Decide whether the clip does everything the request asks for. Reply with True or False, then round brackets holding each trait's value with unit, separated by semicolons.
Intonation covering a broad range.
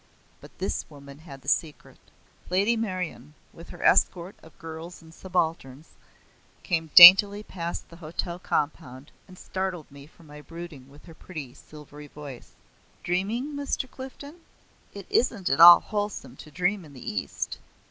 False (4.2 semitones)